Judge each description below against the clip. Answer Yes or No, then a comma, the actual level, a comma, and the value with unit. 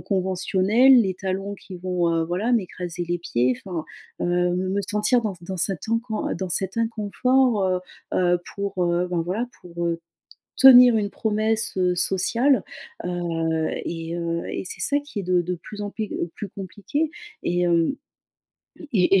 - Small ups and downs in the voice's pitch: No, average, 3.5 semitones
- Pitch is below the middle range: No, medium, 185 Hz